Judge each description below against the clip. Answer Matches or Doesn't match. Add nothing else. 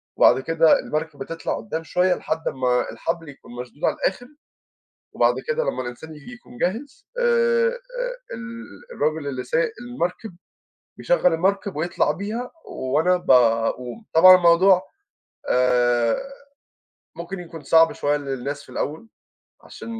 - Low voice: Doesn't match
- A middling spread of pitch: Doesn't match